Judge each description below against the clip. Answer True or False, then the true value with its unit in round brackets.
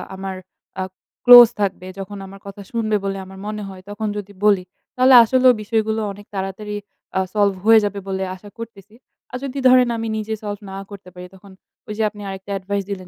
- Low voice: False (205 Hz)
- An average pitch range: False (2.3 semitones)